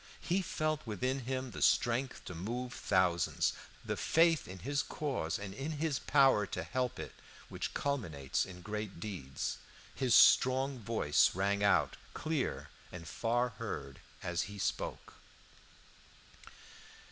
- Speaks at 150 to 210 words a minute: No, slow, 135 wpm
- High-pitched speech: No, low, 115 Hz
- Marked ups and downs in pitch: Yes, wide, 6.2 semitones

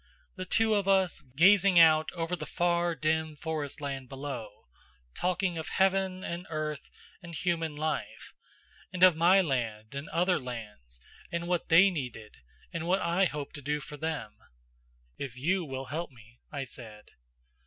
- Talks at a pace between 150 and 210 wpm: Yes, average, 155 wpm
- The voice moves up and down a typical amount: Yes, average, 4.7 semitones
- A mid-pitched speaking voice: Yes, medium, 160 Hz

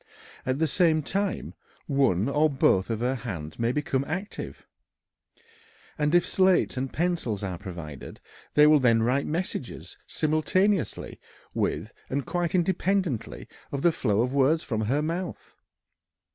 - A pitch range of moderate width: No, wide, 6.5 semitones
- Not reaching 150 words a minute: Yes, average, 140 wpm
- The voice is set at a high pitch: No, medium, 140 Hz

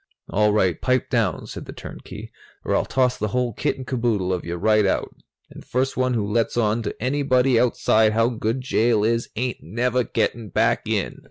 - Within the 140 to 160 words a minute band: No, average, 195 wpm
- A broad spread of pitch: No, average, 2.8 semitones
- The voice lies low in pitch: Yes, low, 115 Hz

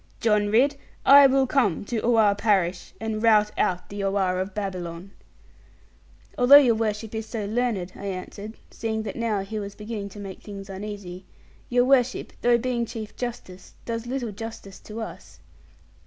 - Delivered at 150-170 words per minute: Yes, average, 165 wpm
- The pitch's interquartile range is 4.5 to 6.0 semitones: No, average, 2.9 semitones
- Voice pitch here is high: Yes, high, 215 Hz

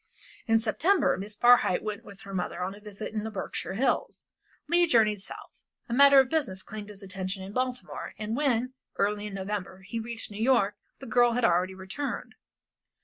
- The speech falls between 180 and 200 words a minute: Yes, average, 190 wpm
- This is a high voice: Yes, high, 215 Hz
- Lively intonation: No, average, 3.9 semitones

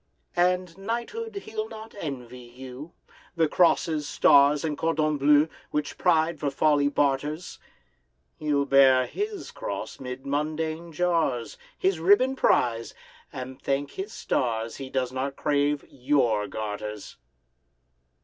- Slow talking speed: Yes, slow, 120 wpm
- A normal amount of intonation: Yes, average, 4.2 semitones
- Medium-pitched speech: Yes, medium, 145 Hz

